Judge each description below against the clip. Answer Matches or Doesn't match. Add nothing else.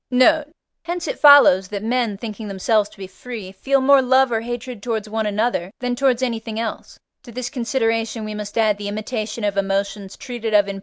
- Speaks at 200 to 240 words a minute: Matches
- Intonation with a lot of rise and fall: Doesn't match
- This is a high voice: Matches